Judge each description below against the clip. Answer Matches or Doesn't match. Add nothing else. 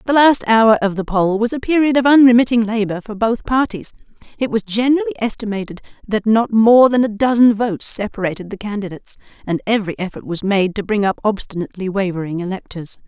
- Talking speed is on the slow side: Doesn't match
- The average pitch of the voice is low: Doesn't match